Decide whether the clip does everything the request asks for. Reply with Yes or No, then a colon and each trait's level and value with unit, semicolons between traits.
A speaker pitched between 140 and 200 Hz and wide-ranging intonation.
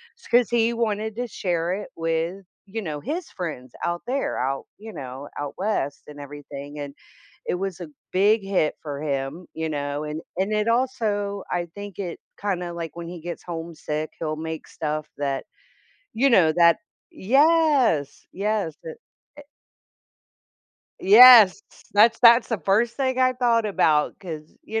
Yes: medium, 185 Hz; wide, 6.4 semitones